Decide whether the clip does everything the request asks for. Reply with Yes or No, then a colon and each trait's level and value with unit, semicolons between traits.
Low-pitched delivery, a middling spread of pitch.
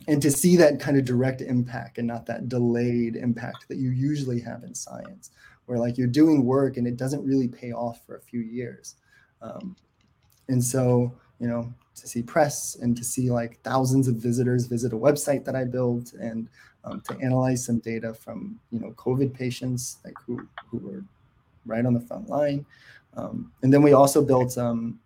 No: low, 125 Hz; narrow, 2.1 semitones